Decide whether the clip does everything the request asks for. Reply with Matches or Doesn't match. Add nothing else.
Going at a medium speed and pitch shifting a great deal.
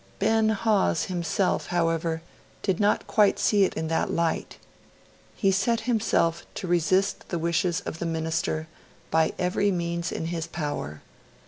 Doesn't match